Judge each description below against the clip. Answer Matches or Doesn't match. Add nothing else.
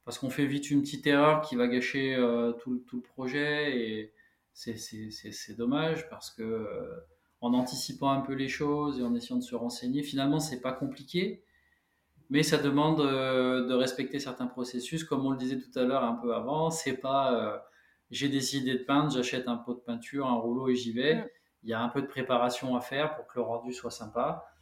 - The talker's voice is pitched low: Matches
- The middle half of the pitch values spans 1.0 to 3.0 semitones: Matches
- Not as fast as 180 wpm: Doesn't match